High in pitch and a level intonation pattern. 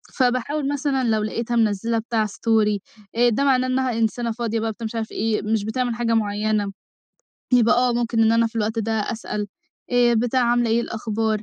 Yes: high, 230 Hz; narrow, 1.7 semitones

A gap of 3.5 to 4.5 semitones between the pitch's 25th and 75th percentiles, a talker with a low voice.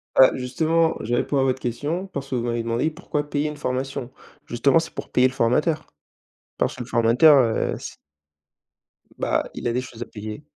Yes: average, 3.8 semitones; low, 130 Hz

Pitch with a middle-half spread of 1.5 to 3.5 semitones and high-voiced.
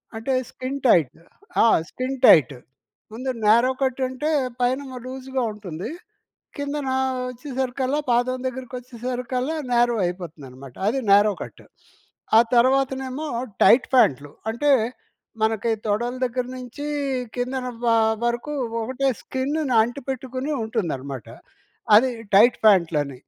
Yes: average, 3.2 semitones; very high, 250 Hz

